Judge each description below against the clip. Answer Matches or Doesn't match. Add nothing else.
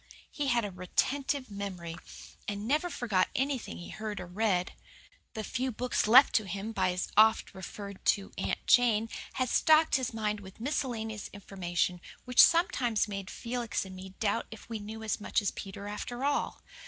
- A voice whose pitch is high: Matches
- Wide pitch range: Doesn't match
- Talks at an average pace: Matches